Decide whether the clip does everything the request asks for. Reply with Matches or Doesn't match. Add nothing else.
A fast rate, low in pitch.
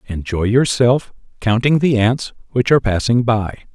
Doesn't match